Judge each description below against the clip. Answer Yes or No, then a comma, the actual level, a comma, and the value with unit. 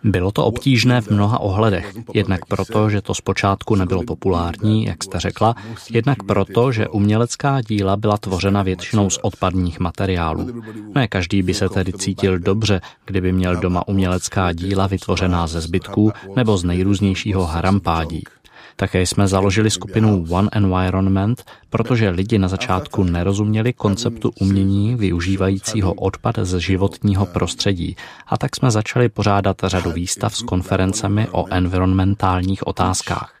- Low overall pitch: Yes, very low, 95 Hz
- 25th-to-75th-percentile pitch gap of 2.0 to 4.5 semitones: Yes, narrow, 2.6 semitones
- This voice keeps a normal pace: Yes, average, 135 wpm